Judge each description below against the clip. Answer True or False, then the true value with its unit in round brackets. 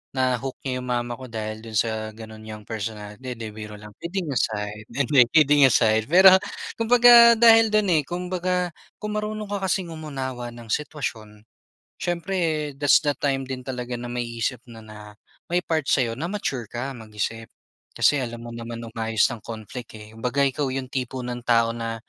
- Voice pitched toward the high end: False (125 Hz)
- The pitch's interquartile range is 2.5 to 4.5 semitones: False (5.5 semitones)